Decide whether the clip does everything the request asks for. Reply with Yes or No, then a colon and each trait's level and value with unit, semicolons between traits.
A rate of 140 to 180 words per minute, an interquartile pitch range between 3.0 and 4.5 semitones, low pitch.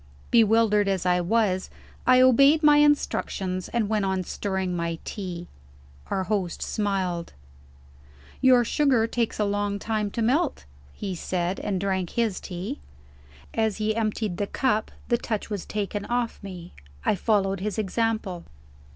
No: average, 145 wpm; average, 3.3 semitones; high, 205 Hz